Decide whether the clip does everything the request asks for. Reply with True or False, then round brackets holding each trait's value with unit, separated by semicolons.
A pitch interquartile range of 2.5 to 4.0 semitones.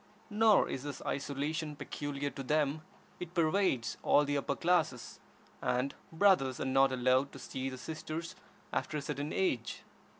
True (3.1 semitones)